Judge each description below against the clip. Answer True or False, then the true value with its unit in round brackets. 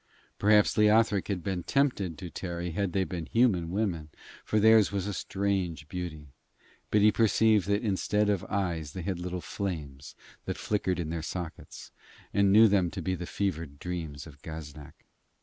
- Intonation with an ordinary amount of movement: True (3.6 semitones)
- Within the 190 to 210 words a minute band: False (170 wpm)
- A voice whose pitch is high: False (95 Hz)